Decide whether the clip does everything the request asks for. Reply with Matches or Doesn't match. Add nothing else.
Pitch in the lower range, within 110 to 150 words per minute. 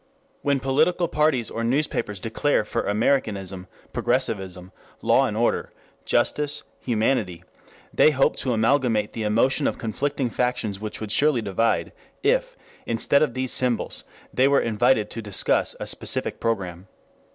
Matches